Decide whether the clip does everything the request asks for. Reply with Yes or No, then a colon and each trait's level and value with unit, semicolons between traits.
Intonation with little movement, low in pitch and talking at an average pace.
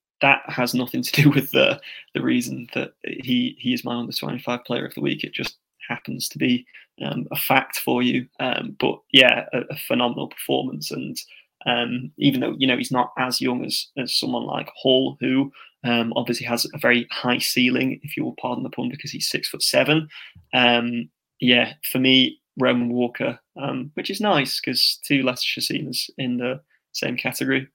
Yes: narrow, 2.1 semitones; low, 125 Hz; average, 190 wpm